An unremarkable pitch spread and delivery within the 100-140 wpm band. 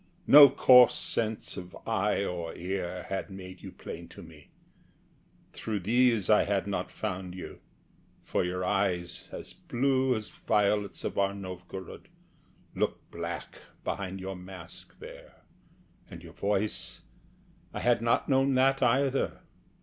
Yes: average, 4.2 semitones; slow, 135 wpm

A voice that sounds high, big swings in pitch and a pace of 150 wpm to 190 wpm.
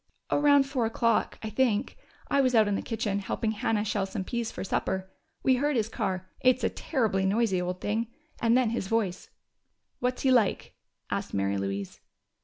No: high, 220 Hz; average, 4.4 semitones; average, 185 wpm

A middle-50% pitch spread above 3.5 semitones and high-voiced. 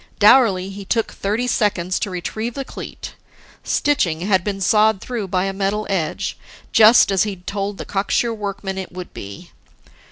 No: narrow, 2.5 semitones; high, 200 Hz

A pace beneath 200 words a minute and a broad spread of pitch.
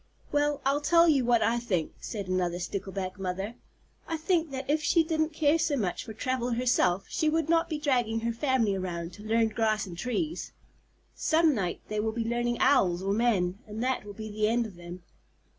No: fast, 205 wpm; wide, 6.7 semitones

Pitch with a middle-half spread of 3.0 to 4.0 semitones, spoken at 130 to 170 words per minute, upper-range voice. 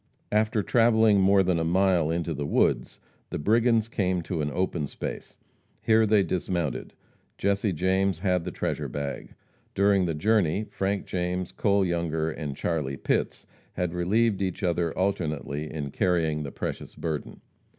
No: average, 3.7 semitones; average, 150 wpm; very low, 90 Hz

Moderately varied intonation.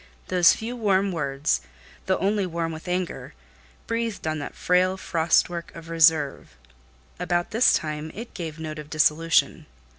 Yes: average, 3.1 semitones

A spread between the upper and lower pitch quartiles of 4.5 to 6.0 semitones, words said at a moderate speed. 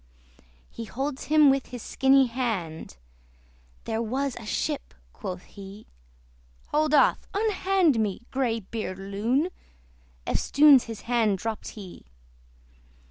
No: average, 4.8 semitones; slow, 115 wpm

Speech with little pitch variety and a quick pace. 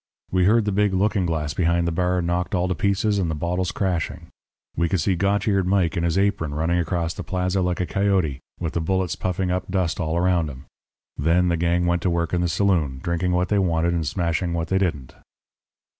Yes: narrow, 2.0 semitones; fast, 225 wpm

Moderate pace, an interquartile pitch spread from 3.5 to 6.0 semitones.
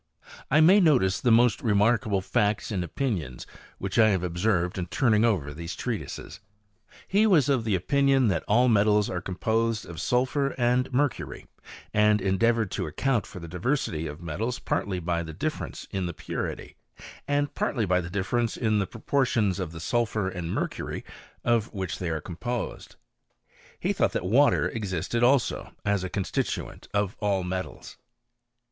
Yes: average, 160 wpm; average, 5.0 semitones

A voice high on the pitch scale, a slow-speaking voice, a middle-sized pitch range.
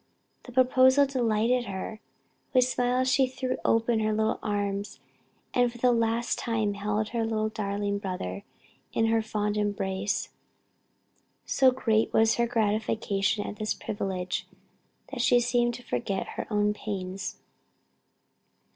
Yes: high, 220 Hz; slow, 130 wpm; average, 3.0 semitones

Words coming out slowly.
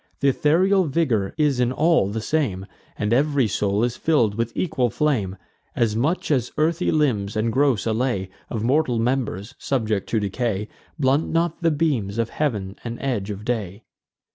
No: average, 165 wpm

